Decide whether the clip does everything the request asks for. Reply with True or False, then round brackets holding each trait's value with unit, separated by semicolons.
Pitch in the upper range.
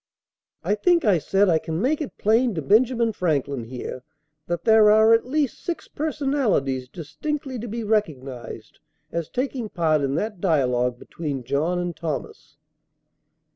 True (195 Hz)